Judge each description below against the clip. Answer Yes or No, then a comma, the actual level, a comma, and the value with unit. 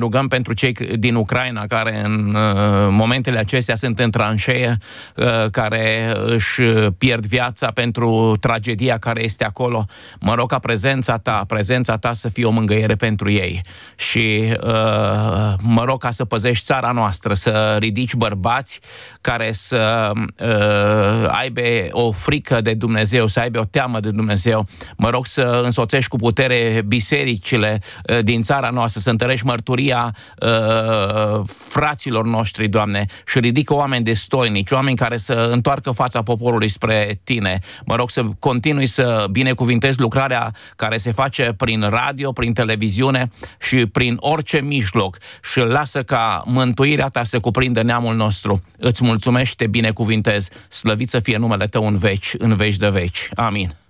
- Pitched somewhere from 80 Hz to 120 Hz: Yes, low, 115 Hz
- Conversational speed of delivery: Yes, average, 150 wpm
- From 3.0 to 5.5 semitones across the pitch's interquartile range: No, narrow, 2.5 semitones